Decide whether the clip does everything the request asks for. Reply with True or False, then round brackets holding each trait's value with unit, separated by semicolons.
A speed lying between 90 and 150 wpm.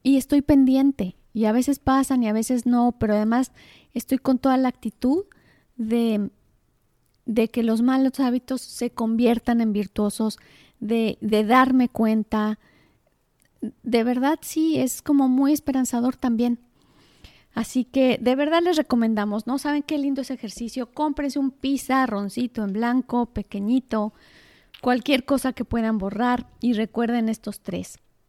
True (145 wpm)